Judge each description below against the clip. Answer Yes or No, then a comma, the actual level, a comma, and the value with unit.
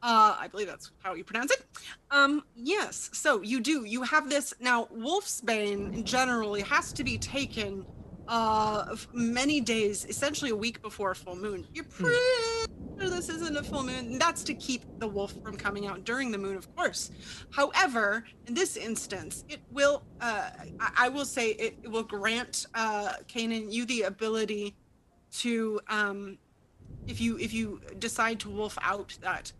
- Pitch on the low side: No, high, 225 Hz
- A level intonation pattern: No, average, 4.8 semitones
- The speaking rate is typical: Yes, average, 175 wpm